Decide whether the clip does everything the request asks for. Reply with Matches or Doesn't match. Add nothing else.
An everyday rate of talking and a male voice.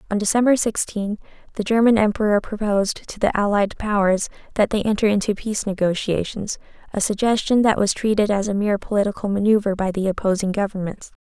Doesn't match